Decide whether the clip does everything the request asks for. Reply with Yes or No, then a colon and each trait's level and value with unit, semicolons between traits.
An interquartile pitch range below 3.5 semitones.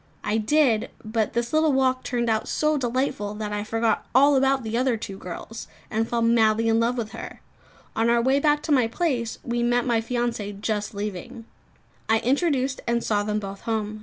Yes: average, 3.0 semitones